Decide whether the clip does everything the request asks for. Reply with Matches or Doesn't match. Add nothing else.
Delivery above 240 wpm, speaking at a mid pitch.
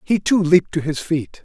Matches